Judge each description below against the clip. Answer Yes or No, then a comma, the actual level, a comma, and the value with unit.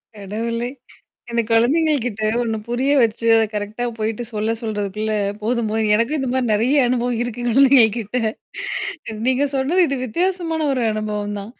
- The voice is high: Yes, high, 235 Hz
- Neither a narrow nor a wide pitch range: Yes, average, 3.3 semitones